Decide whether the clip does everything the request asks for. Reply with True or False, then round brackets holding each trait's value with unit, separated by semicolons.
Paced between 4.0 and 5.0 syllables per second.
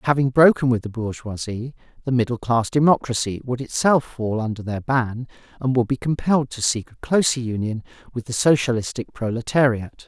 False (5.4 syllables/s)